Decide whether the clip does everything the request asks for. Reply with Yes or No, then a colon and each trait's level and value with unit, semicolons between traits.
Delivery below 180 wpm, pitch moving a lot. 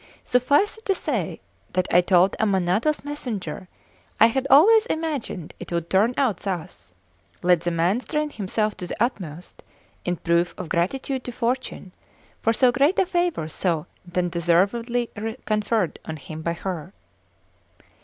Yes: average, 145 wpm; wide, 6.9 semitones